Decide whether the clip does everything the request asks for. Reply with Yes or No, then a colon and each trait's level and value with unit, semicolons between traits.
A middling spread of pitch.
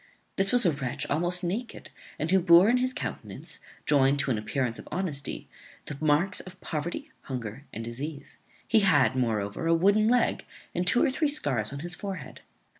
No: wide, 6.3 semitones